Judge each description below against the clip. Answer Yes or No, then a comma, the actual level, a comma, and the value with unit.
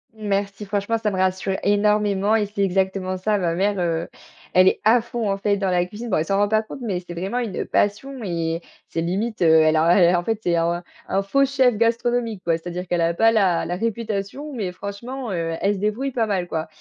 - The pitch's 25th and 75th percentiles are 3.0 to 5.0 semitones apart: Yes, average, 3.7 semitones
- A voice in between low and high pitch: No, high, 200 Hz